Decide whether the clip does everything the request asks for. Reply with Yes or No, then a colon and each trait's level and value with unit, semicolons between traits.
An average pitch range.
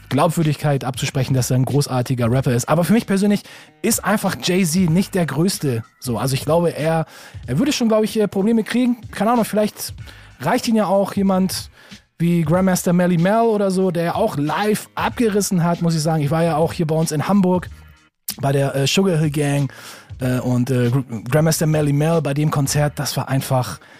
No: wide, 6.2 semitones